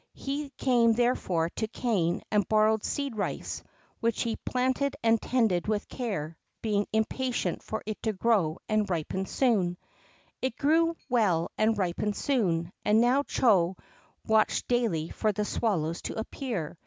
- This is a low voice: No, high, 220 Hz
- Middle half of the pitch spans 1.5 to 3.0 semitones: No, average, 4.4 semitones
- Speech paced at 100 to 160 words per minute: Yes, average, 145 wpm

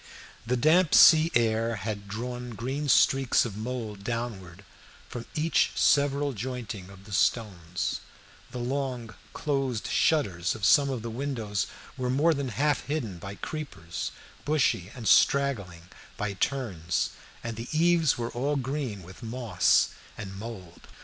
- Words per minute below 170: Yes, average, 140 wpm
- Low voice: Yes, low, 120 Hz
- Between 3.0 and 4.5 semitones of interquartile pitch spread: No, average, 5.3 semitones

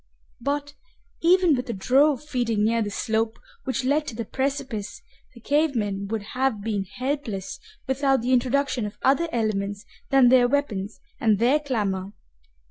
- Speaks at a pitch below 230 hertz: No, high, 245 Hz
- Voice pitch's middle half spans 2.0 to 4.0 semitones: No, average, 4.6 semitones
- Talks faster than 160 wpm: No, average, 155 wpm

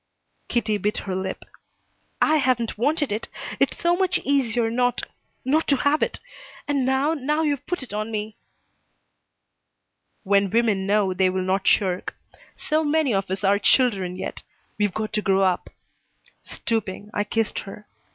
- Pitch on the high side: Yes, high, 220 Hz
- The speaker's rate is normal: Yes, average, 160 wpm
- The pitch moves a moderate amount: No, wide, 5.8 semitones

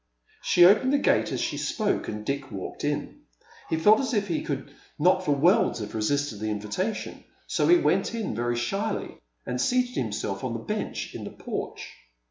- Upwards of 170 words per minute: Yes, average, 190 wpm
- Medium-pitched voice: Yes, medium, 145 Hz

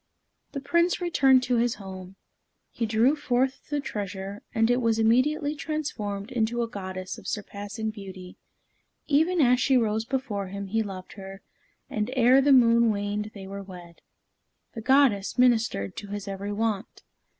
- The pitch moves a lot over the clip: No, average, 4.4 semitones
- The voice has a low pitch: No, high, 225 Hz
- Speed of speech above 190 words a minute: No, average, 160 wpm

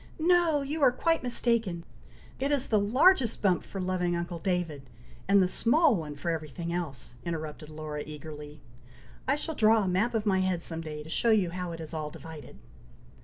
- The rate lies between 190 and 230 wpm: Yes, average, 195 wpm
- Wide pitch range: Yes, wide, 6.7 semitones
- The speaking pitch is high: No, medium, 180 Hz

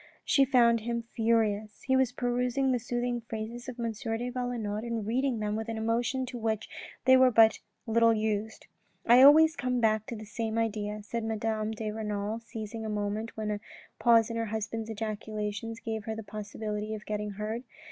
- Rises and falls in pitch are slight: Yes, narrow, 2.0 semitones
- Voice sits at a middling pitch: No, high, 225 Hz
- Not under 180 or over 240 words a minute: Yes, average, 190 wpm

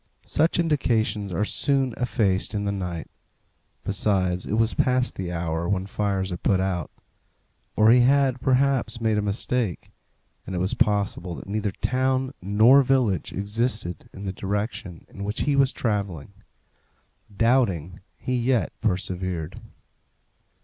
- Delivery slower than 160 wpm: Yes, average, 140 wpm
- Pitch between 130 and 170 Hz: No, low, 105 Hz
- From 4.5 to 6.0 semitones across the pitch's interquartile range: Yes, average, 5.0 semitones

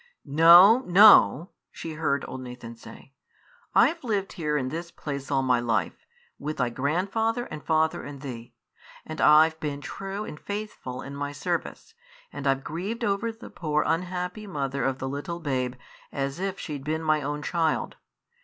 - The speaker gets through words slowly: No, average, 165 wpm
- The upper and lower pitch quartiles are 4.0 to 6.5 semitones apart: Yes, average, 4.8 semitones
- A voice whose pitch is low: No, medium, 155 Hz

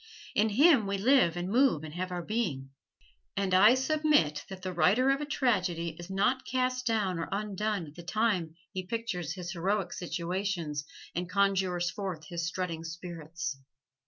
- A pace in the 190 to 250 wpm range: No, average, 165 wpm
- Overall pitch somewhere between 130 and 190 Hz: Yes, medium, 185 Hz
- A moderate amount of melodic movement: Yes, average, 4.1 semitones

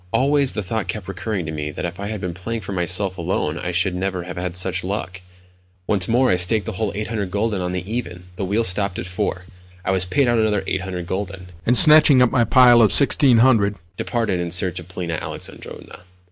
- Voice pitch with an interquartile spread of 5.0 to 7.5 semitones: No, average, 3.8 semitones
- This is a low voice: Yes, very low, 95 Hz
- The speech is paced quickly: Yes, fast, 215 wpm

